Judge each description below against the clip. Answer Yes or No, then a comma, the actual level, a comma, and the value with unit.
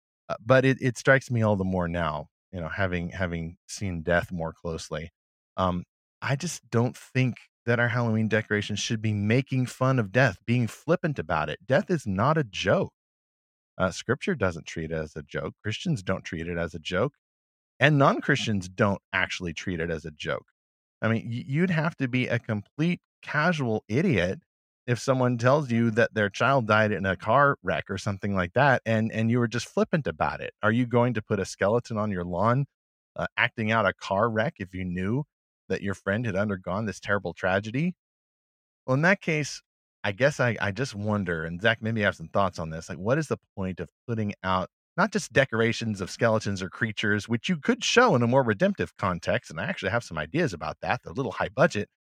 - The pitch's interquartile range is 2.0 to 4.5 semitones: No, average, 5.3 semitones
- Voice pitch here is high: No, low, 110 Hz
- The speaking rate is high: Yes, fast, 210 wpm